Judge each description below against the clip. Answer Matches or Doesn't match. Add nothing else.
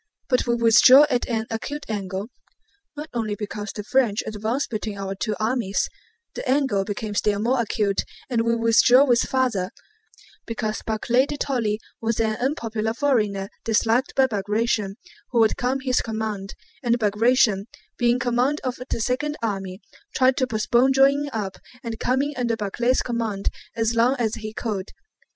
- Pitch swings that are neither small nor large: Matches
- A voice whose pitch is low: Doesn't match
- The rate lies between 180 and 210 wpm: Doesn't match